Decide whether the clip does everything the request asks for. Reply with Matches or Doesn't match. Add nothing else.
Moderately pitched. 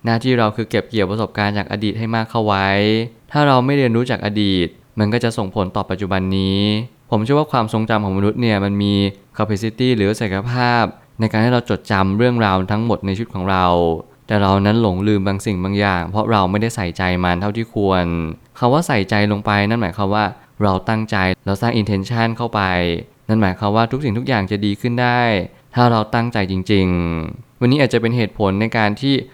Doesn't match